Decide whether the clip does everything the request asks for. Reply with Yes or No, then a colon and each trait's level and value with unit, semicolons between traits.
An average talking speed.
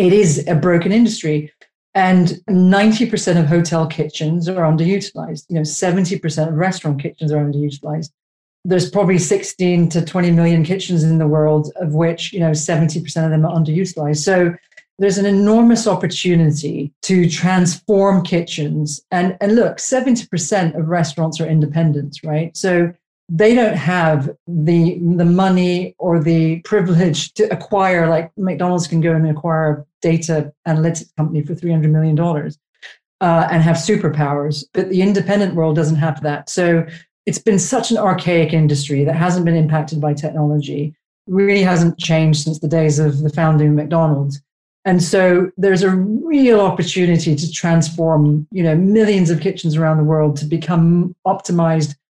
Yes: average, 155 wpm